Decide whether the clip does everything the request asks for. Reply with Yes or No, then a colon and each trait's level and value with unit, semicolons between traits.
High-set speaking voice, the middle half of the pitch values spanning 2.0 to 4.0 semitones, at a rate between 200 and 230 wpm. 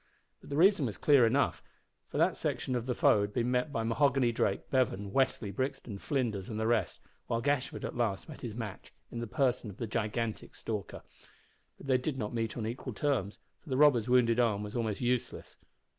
No: low, 120 Hz; average, 3.1 semitones; fast, 205 wpm